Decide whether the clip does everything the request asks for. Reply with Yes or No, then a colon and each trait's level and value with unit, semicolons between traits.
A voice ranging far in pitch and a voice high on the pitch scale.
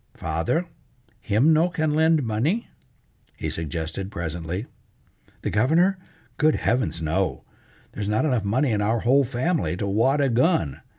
No: wide, 7.9 semitones; low, 115 Hz